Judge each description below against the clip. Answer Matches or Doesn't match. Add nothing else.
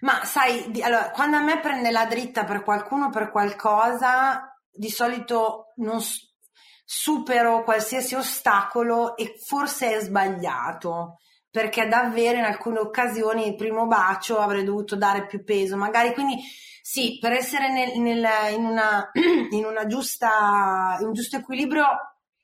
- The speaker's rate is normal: Matches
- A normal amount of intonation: Matches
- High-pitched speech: Matches